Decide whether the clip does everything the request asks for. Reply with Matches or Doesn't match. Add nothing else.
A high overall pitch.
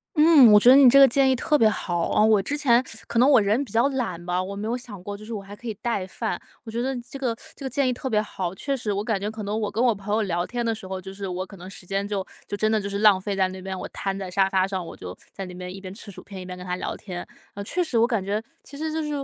Matches